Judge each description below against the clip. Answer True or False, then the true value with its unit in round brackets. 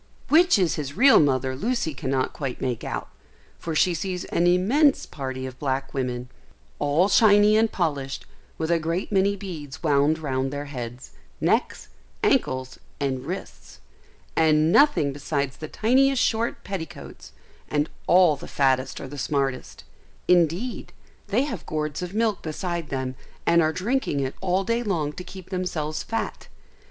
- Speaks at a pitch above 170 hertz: False (160 Hz)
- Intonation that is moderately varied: False (5.8 semitones)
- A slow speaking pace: False (155 wpm)